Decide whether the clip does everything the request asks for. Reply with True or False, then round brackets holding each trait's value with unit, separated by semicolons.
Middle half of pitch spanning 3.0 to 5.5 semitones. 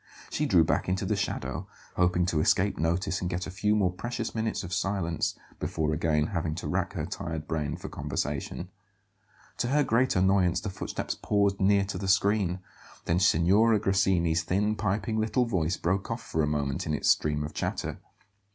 True (4.0 semitones)